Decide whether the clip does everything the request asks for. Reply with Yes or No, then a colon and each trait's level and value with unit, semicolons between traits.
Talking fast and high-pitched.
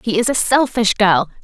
Yes: fast, 210 wpm; high, 220 Hz